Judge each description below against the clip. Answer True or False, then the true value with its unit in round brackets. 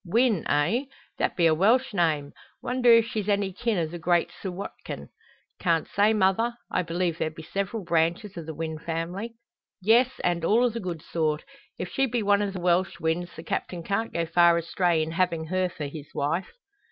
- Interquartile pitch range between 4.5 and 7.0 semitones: False (4.0 semitones)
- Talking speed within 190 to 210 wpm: True (200 wpm)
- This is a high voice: False (180 Hz)